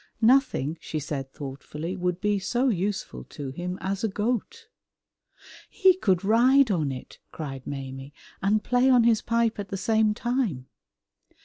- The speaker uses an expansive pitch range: Yes, wide, 7.4 semitones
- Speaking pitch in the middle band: No, high, 200 Hz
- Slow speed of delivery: No, average, 150 wpm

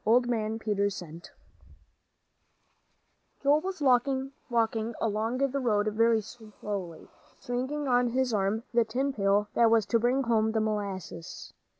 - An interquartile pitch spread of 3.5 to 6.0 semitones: No, average, 2.9 semitones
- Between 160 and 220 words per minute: No, slow, 135 wpm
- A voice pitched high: Yes, high, 225 Hz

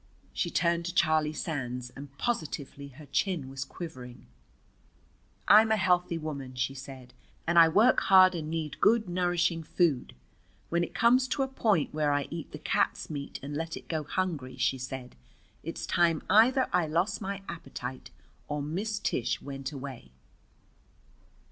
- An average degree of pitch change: Yes, average, 4.5 semitones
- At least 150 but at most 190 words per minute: Yes, average, 160 wpm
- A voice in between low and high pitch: Yes, medium, 160 Hz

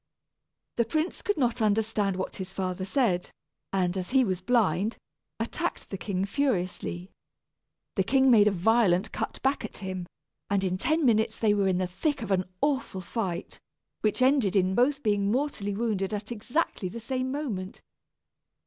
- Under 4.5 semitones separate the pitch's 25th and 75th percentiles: No, average, 4.8 semitones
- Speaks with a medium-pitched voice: No, high, 210 Hz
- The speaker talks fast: No, average, 165 wpm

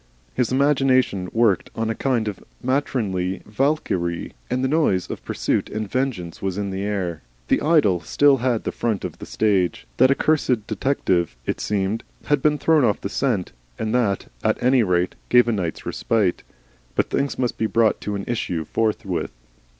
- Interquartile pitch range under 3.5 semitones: No, average, 5.3 semitones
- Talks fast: No, average, 175 wpm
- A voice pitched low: Yes, low, 110 Hz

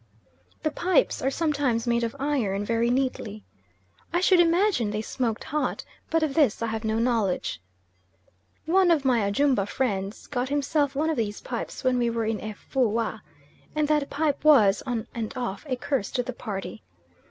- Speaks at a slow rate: No, average, 175 wpm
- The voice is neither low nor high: No, very high, 250 Hz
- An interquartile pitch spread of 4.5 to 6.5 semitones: Yes, average, 4.9 semitones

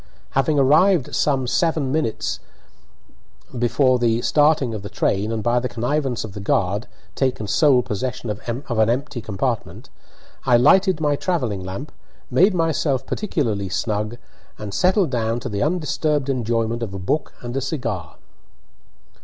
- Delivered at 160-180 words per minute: No, average, 145 wpm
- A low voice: Yes, low, 125 Hz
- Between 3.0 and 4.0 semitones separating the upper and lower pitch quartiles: No, average, 5.1 semitones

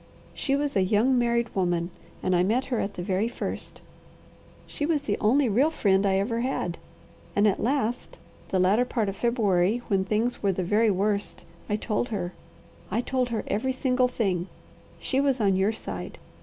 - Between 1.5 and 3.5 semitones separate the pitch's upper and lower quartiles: No, average, 4.4 semitones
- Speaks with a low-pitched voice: No, high, 215 Hz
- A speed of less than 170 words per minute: No, average, 185 wpm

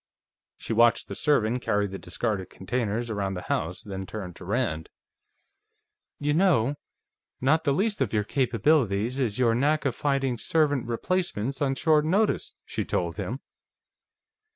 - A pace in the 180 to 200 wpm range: No, average, 150 wpm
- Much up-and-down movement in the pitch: Yes, wide, 5.9 semitones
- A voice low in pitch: Yes, low, 120 Hz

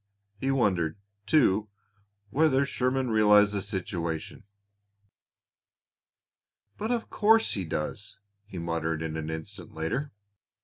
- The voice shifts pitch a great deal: Yes, wide, 8.2 semitones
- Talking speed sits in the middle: No, slow, 100 wpm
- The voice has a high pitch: No, low, 105 Hz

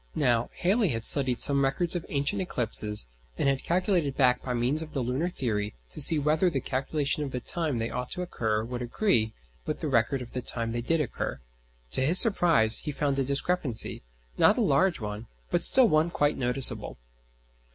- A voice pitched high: No, low, 135 Hz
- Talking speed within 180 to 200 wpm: Yes, average, 195 wpm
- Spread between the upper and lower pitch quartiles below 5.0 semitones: No, average, 5.3 semitones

